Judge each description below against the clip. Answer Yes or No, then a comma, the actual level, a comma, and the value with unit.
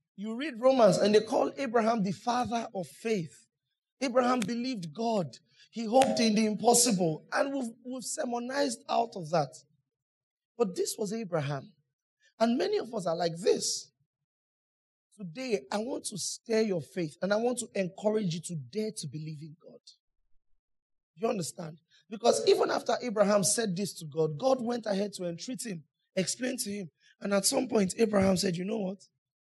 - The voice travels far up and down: Yes, wide, 6.5 semitones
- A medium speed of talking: Yes, average, 170 wpm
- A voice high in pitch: Yes, high, 205 Hz